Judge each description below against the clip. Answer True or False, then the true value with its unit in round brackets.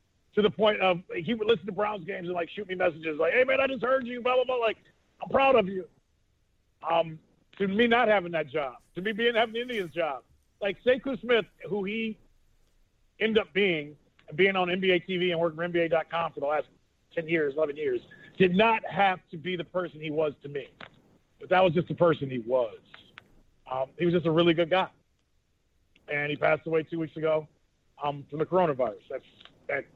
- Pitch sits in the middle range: True (180 Hz)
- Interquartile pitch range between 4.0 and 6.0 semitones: True (5.3 semitones)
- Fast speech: True (215 wpm)